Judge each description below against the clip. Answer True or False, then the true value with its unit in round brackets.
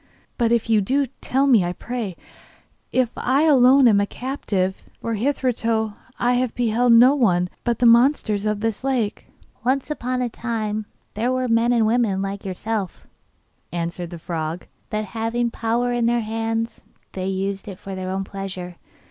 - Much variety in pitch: False (3.8 semitones)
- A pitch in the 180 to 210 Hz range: False (225 Hz)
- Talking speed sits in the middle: True (170 wpm)